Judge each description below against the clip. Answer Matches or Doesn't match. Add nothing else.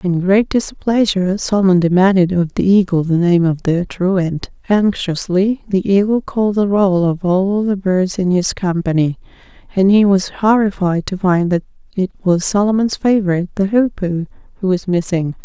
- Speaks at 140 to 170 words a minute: Matches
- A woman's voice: Matches